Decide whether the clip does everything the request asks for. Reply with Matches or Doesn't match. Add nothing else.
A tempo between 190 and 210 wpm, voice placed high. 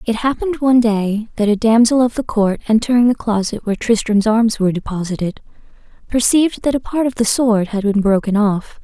Matches